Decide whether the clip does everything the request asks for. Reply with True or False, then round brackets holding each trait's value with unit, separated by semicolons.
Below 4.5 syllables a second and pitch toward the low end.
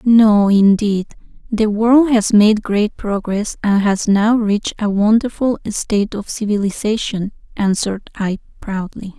False (4.1 syllables/s; 210 Hz)